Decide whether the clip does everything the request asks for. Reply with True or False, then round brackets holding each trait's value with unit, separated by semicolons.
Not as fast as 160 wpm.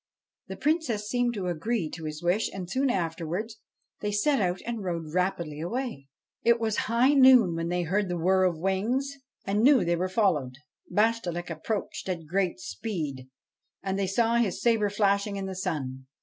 False (180 wpm)